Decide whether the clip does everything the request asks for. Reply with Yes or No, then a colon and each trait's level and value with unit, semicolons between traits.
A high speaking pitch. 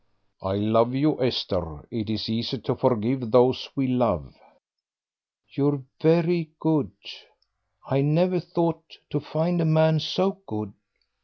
No: low, 135 Hz